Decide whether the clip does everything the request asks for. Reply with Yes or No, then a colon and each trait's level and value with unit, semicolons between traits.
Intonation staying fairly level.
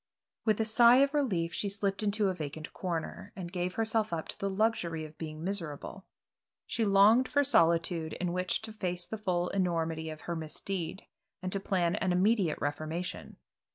No: average, 4.0 semitones